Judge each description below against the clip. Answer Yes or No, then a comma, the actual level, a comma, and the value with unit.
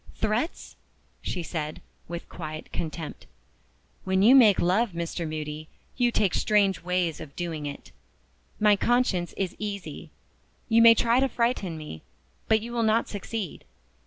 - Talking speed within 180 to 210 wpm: No, average, 145 wpm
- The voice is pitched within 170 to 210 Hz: Yes, high, 190 Hz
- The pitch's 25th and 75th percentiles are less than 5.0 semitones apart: No, wide, 5.5 semitones